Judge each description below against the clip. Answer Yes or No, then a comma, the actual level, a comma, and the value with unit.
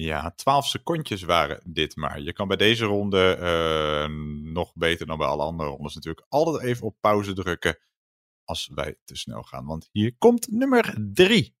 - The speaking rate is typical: Yes, average, 180 wpm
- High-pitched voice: No, very low, 85 Hz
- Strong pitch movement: Yes, wide, 6.0 semitones